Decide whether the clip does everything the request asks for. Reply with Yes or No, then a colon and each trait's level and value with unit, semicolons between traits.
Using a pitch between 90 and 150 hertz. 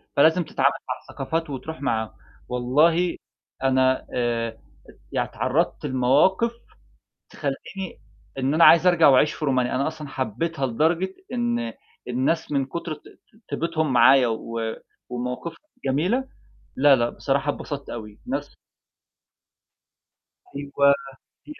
Yes: medium, 140 Hz